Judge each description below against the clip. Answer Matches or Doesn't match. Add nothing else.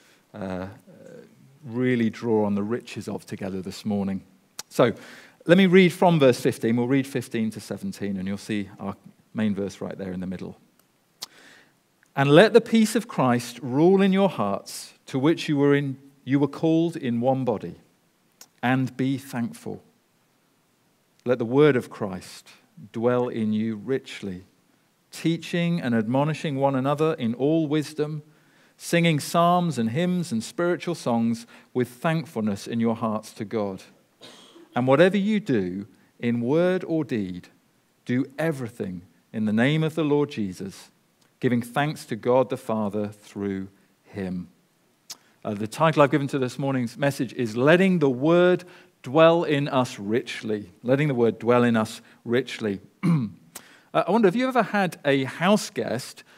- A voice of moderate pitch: Doesn't match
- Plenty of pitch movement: Matches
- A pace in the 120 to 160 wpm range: Matches